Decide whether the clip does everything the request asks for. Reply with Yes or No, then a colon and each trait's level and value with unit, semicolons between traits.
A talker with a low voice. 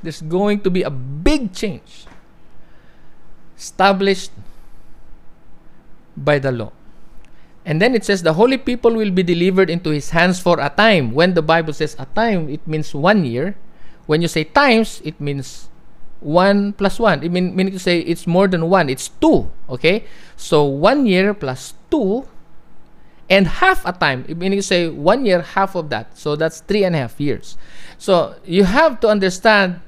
No: medium, 180 Hz